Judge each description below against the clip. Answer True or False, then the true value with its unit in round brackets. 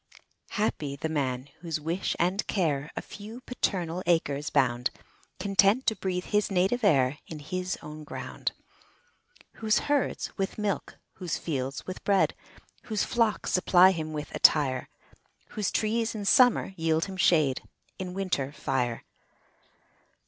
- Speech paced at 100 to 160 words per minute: True (135 wpm)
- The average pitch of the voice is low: False (180 Hz)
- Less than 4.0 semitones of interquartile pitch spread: False (5.3 semitones)